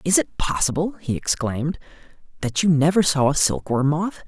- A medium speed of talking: Yes, average, 170 wpm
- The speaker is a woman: No, male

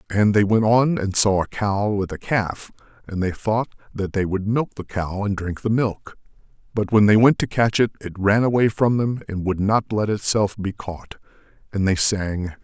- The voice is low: Yes, low, 105 Hz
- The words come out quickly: Yes, fast, 220 wpm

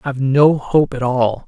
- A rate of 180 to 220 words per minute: No, fast, 245 wpm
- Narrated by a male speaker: Yes, male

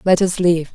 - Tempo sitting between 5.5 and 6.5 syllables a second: No, 4.8 syllables/s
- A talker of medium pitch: Yes, medium, 175 Hz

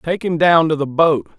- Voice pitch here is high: No, medium, 160 Hz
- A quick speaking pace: Yes, fast, 260 wpm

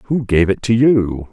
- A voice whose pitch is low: Yes, low, 110 Hz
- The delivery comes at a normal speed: No, fast, 225 wpm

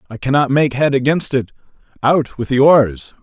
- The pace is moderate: Yes, average, 185 wpm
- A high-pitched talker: No, low, 135 Hz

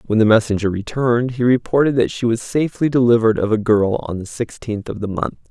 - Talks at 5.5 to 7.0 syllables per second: Yes, 6.1 syllables/s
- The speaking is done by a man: Yes, male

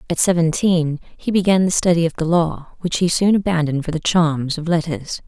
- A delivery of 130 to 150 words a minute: No, fast, 205 wpm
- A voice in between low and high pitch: Yes, medium, 170 Hz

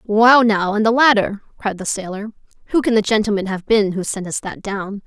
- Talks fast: Yes, fast, 225 wpm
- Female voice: Yes, female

